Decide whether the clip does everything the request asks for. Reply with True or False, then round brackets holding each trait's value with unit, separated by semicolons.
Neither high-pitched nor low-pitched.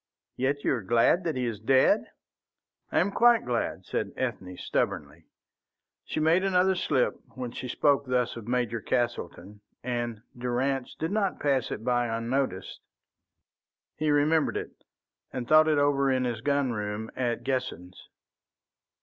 False (125 Hz)